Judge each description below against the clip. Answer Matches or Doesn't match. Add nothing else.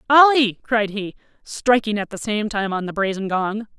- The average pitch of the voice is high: Matches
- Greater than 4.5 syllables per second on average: Matches